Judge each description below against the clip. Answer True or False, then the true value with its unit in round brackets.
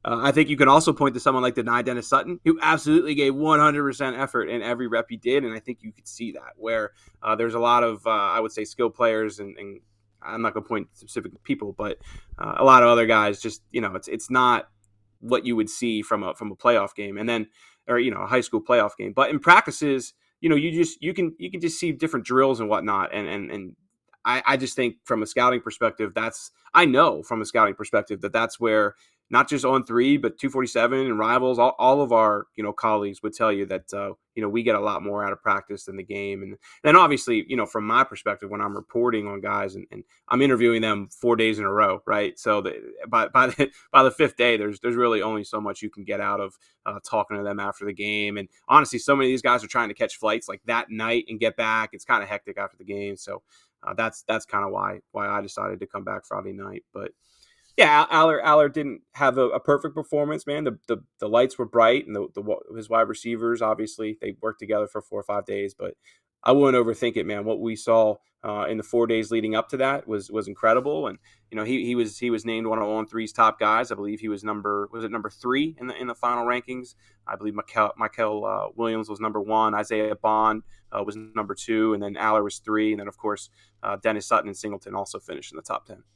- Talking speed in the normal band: False (255 wpm)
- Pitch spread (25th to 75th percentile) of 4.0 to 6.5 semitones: False (3.5 semitones)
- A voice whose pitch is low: True (115 Hz)